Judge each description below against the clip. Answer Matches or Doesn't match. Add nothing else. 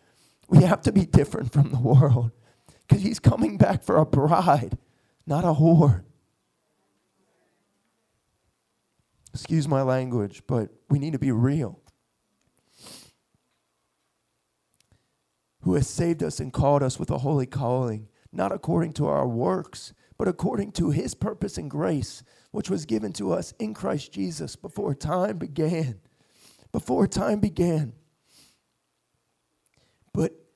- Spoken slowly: Matches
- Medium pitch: Matches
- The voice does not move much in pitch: Doesn't match